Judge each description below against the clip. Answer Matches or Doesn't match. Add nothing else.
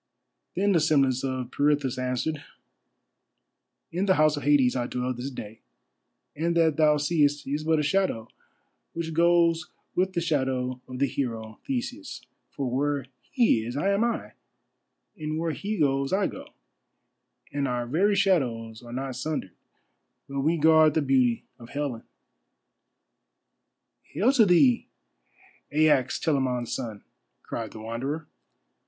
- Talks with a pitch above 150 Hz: Doesn't match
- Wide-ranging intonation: Doesn't match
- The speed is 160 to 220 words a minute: Doesn't match